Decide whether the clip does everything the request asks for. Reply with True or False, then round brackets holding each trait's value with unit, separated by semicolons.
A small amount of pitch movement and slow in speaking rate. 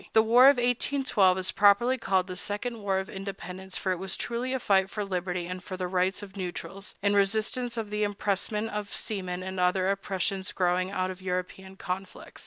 False (2.3 semitones; 195 wpm)